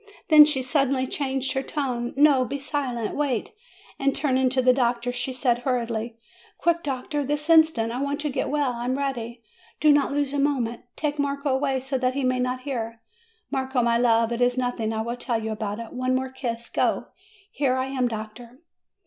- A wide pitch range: No, average, 2.7 semitones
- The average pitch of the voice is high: Yes, very high, 255 Hz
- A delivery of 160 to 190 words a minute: No, average, 200 wpm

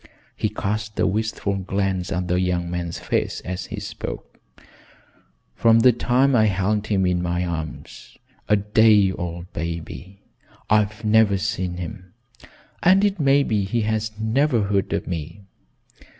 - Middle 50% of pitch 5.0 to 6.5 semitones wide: No, average, 3.5 semitones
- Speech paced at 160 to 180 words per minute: No, average, 150 wpm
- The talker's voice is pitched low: Yes, low, 100 Hz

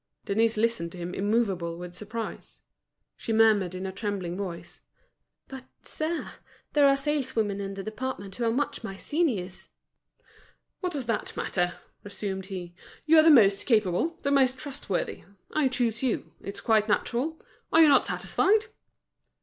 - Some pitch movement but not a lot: No, wide, 5.9 semitones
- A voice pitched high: Yes, high, 220 Hz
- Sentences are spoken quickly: No, average, 155 wpm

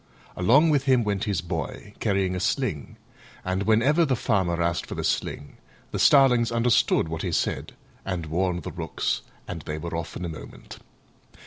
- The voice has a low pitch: Yes, very low, 95 Hz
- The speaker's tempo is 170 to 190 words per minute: Yes, average, 180 wpm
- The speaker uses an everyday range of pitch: No, wide, 5.7 semitones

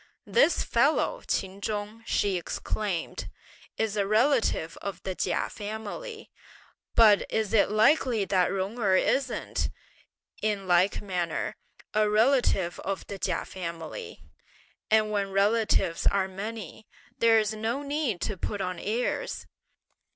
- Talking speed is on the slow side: Yes, slow, 125 wpm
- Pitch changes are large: No, average, 2.9 semitones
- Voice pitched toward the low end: No, high, 210 Hz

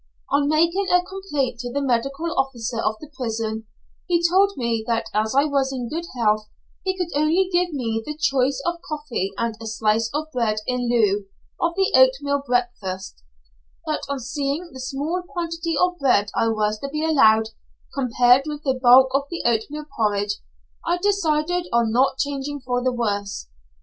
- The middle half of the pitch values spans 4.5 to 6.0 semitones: Yes, average, 5.1 semitones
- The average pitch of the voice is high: Yes, very high, 270 Hz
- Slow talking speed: No, average, 175 wpm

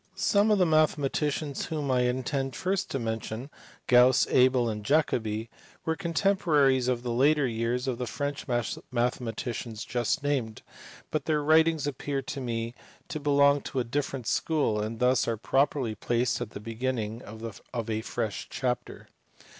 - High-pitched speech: No, low, 130 Hz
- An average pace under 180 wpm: Yes, average, 155 wpm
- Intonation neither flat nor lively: Yes, average, 3.8 semitones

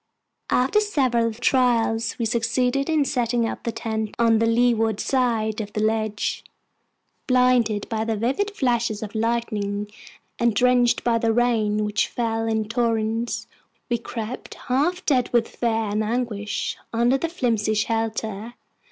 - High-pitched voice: Yes, high, 230 Hz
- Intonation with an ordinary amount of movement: No, narrow, 2.0 semitones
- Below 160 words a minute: Yes, average, 145 wpm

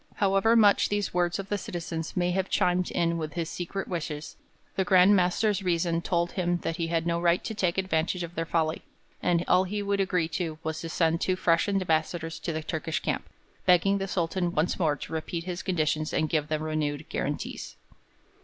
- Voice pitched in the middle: Yes, medium, 175 Hz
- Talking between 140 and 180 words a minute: No, average, 200 wpm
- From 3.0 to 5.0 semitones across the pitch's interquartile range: No, narrow, 2.4 semitones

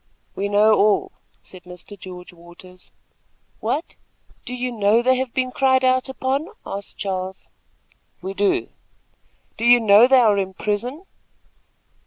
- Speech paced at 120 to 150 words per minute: Yes, average, 140 wpm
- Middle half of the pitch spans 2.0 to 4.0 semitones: No, average, 5.0 semitones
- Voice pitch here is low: No, high, 210 Hz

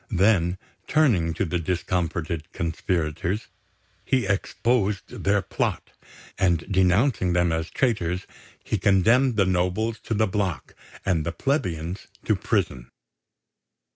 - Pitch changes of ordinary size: Yes, average, 3.9 semitones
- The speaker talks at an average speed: No, slow, 115 wpm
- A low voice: Yes, very low, 95 Hz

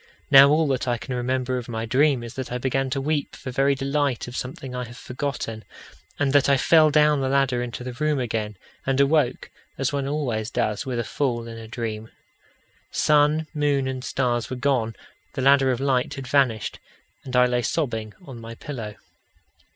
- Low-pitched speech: Yes, low, 130 Hz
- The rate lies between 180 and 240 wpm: Yes, average, 195 wpm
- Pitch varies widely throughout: No, average, 2.7 semitones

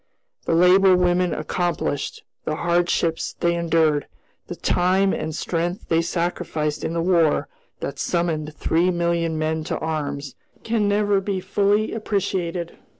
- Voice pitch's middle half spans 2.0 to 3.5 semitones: Yes, narrow, 2.4 semitones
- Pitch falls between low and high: Yes, medium, 170 Hz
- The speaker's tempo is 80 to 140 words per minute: Yes, slow, 135 wpm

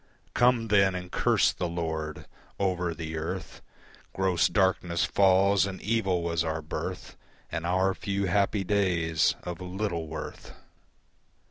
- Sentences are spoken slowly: Yes, slow, 130 wpm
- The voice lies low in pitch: Yes, very low, 90 Hz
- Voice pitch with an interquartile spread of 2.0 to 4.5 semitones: Yes, average, 2.8 semitones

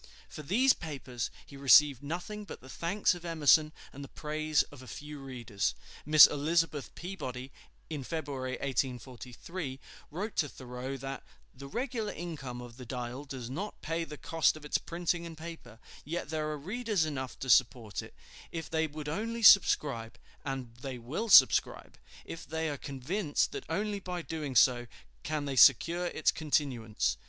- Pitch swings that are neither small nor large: Yes, average, 4.3 semitones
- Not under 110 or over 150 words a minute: No, average, 165 wpm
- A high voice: No, medium, 150 Hz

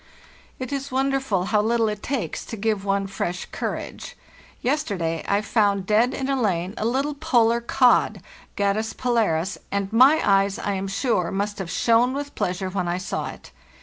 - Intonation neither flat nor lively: Yes, average, 4.3 semitones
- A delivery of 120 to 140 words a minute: No, average, 175 wpm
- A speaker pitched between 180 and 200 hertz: No, high, 215 Hz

